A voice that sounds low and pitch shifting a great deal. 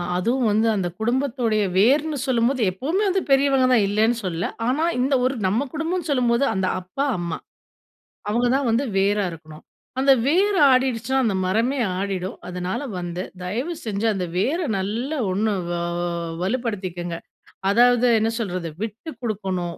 No: high, 230 Hz; wide, 5.8 semitones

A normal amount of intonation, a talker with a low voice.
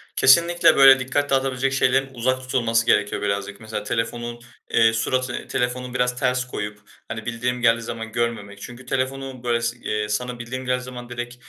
No: narrow, 2.1 semitones; low, 125 Hz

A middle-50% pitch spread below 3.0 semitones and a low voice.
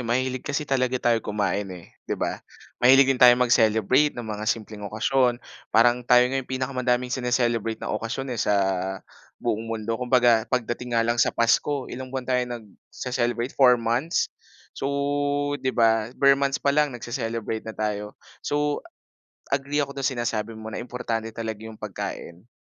Yes: narrow, 2.6 semitones; low, 120 Hz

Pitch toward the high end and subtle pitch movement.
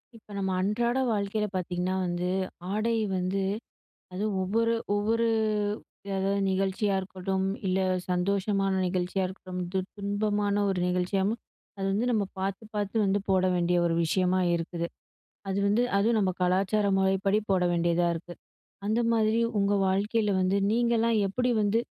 Yes: high, 195 Hz; narrow, 2.3 semitones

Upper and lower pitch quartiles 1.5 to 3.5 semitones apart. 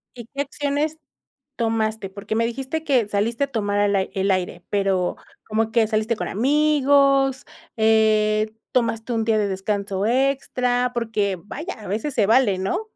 No: average, 4.4 semitones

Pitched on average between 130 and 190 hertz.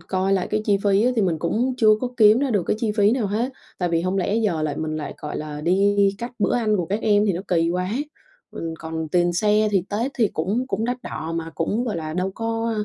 No: high, 200 Hz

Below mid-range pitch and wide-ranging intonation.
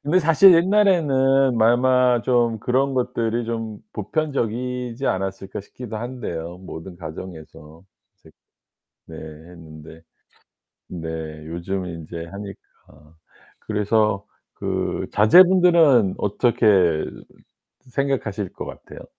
Yes: low, 110 Hz; wide, 6.5 semitones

